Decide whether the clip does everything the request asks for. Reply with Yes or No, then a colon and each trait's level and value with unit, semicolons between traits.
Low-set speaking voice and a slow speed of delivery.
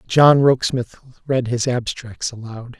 Yes: low, 125 Hz; slow, 130 wpm